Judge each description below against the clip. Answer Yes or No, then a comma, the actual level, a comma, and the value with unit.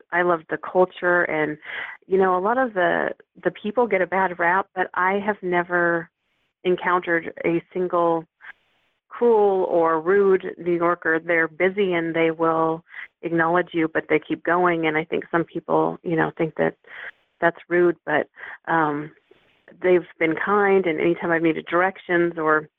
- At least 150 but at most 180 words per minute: Yes, average, 165 wpm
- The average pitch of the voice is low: No, medium, 175 Hz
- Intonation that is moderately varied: No, narrow, 2.1 semitones